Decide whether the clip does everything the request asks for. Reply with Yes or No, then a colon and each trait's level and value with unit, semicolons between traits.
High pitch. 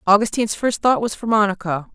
Yes: high, 210 Hz